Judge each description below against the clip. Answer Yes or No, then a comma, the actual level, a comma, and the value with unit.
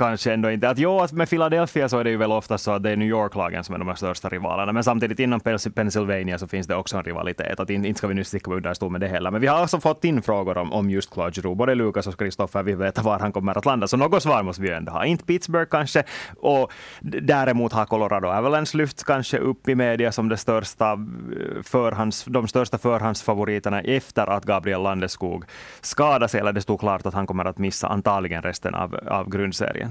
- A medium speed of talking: No, fast, 235 wpm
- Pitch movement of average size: Yes, average, 4.3 semitones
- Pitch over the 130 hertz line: No, low, 105 Hz